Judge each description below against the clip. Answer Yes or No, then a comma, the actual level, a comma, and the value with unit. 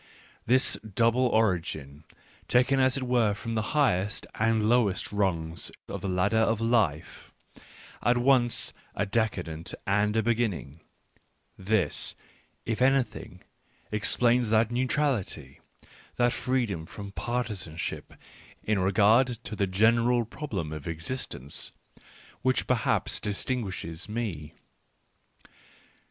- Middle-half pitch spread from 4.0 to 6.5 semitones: Yes, average, 4.4 semitones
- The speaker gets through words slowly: Yes, slow, 115 wpm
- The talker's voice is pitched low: Yes, low, 110 Hz